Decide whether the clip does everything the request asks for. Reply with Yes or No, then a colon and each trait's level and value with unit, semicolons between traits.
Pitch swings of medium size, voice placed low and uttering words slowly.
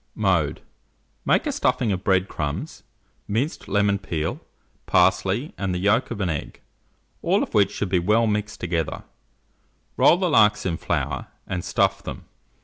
No: average, 3.5 semitones; low, 100 Hz; average, 155 wpm